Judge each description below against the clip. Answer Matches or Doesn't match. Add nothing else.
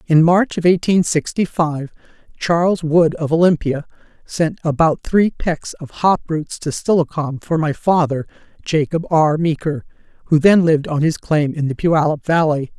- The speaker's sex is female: Matches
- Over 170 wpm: Doesn't match